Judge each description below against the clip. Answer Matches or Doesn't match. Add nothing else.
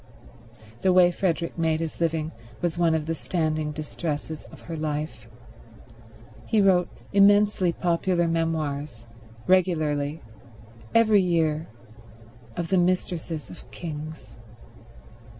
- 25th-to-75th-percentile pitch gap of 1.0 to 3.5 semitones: Matches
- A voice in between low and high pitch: Matches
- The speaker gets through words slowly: Matches